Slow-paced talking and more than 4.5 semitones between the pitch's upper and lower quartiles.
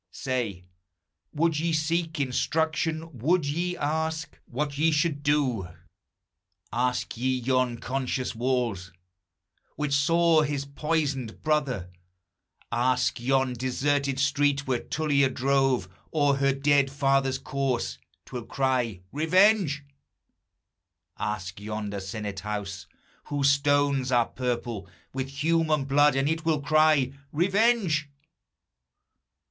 No: slow, 110 wpm; average, 3.4 semitones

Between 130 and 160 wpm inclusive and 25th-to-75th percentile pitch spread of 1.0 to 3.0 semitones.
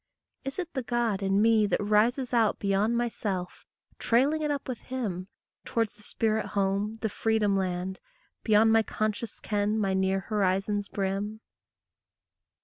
Yes: average, 150 wpm; average, 2.7 semitones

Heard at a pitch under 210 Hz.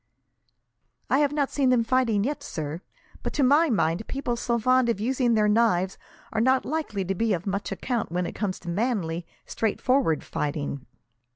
No: high, 225 Hz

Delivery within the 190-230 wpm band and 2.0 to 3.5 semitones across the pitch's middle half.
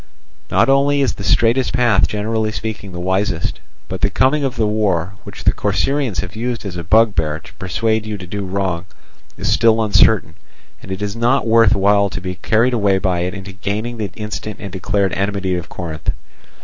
Yes: average, 195 wpm; average, 3.2 semitones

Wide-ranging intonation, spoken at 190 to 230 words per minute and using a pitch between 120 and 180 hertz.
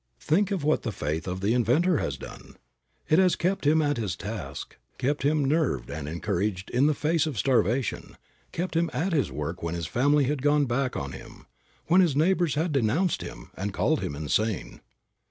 Yes: wide, 8.1 semitones; average, 195 wpm; low, 135 Hz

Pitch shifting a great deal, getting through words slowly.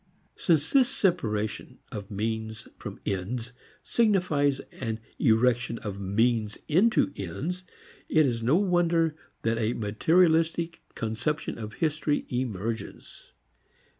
Yes: wide, 6.9 semitones; slow, 105 wpm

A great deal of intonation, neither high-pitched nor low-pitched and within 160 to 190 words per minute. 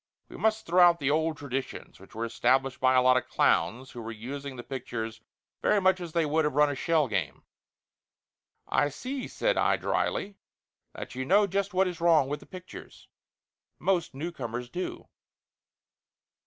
Yes: wide, 5.7 semitones; medium, 145 Hz; average, 175 wpm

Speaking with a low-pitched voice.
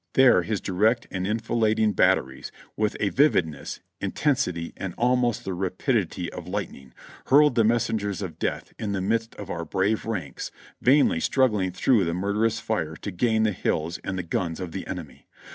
Yes: low, 105 Hz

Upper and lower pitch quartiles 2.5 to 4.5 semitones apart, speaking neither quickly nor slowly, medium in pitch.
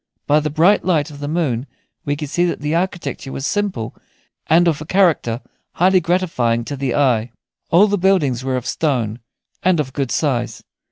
No: average, 5.1 semitones; average, 185 wpm; medium, 150 Hz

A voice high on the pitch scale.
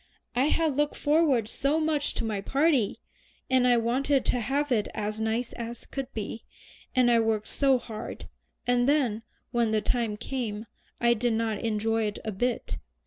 Yes: high, 235 Hz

